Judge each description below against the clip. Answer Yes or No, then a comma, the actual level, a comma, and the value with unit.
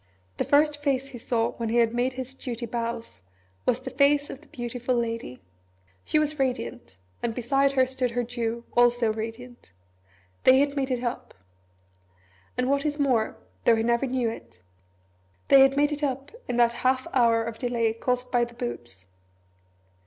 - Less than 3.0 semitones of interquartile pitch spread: Yes, narrow, 2.5 semitones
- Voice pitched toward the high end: Yes, high, 245 Hz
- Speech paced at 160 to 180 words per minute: Yes, average, 175 wpm